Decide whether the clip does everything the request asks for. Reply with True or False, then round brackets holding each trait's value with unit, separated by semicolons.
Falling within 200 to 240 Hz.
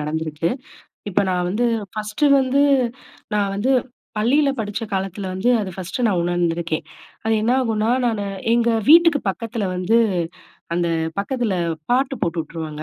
True (205 Hz)